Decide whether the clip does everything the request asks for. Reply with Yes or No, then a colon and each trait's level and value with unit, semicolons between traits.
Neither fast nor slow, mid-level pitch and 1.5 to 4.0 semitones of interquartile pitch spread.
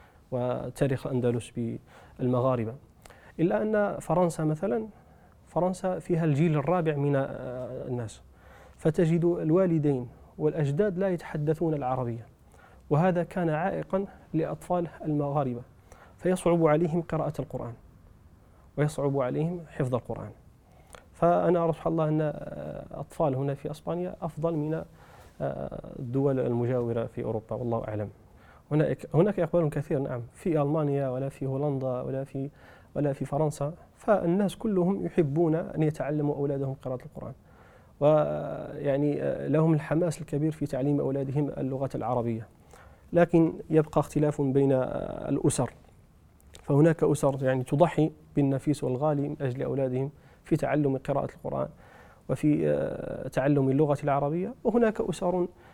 No: average, 110 wpm; medium, 145 Hz; average, 4.4 semitones